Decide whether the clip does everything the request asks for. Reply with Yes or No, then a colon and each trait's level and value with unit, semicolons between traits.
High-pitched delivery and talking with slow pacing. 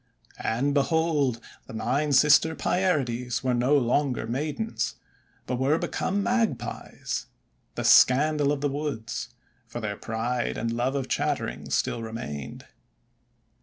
No: low, 135 Hz; slow, 130 wpm